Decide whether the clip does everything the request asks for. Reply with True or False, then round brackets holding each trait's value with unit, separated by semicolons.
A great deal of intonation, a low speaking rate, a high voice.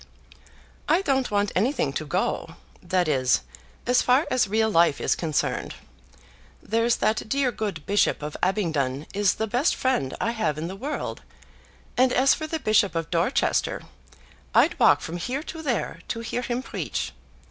False (6.7 semitones; 165 wpm; 215 Hz)